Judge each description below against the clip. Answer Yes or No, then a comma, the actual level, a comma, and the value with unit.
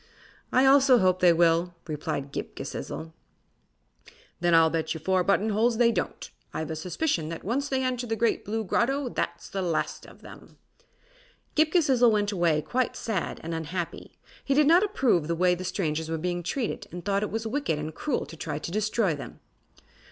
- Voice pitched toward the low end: No, high, 190 Hz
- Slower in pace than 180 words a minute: No, average, 190 wpm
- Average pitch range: No, wide, 6.6 semitones